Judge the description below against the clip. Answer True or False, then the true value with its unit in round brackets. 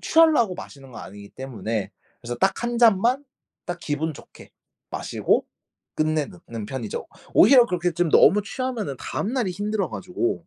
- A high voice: False (180 Hz)